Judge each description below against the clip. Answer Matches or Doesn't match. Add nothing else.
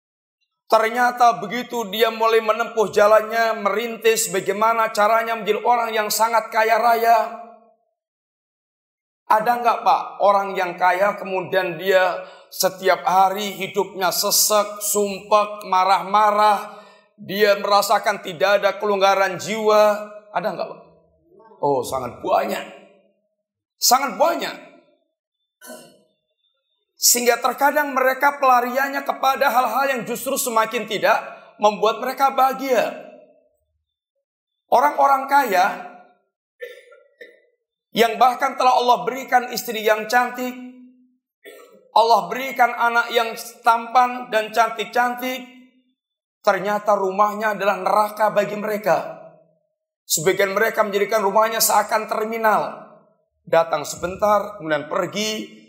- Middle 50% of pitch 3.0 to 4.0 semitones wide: Matches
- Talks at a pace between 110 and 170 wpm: Doesn't match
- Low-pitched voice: Doesn't match